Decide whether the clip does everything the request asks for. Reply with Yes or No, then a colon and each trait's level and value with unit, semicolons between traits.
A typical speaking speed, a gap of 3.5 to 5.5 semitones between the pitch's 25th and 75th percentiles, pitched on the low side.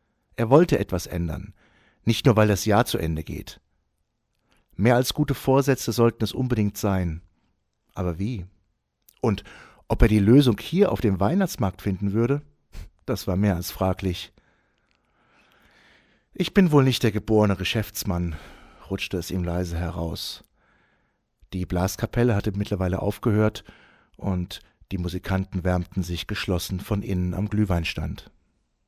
Yes: average, 135 wpm; average, 4.3 semitones; low, 100 Hz